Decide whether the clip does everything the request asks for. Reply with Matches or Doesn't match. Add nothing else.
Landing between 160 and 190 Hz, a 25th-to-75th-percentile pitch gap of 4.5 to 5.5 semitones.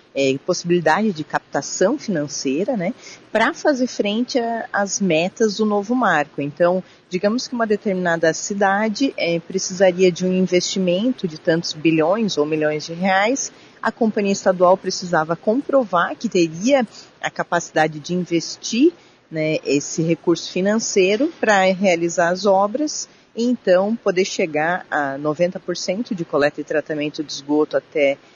Matches